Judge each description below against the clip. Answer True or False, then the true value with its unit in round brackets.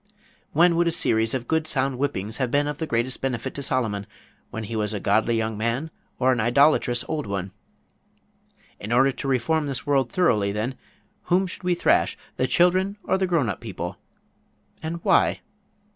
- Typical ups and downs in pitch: False (6.0 semitones)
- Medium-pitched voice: False (130 Hz)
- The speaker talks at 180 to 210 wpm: True (185 wpm)